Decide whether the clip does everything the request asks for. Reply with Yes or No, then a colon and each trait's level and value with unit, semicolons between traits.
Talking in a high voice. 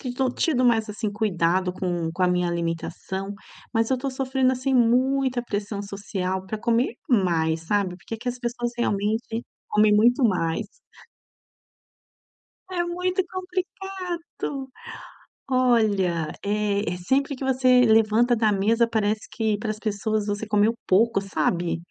Yes: high, 220 Hz